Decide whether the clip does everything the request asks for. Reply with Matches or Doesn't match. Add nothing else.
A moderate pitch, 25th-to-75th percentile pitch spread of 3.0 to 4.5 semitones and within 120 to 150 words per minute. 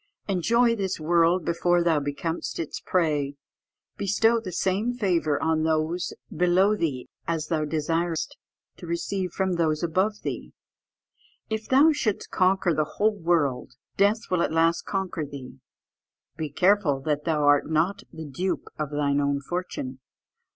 Matches